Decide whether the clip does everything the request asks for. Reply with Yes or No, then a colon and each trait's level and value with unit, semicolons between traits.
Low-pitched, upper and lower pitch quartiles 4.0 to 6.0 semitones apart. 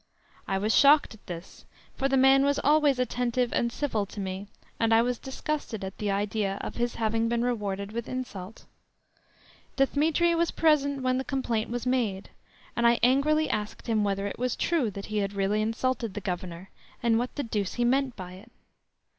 No: high, 235 Hz; average, 4.6 semitones